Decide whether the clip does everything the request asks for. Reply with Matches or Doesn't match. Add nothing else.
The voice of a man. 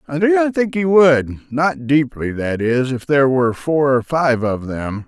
Matches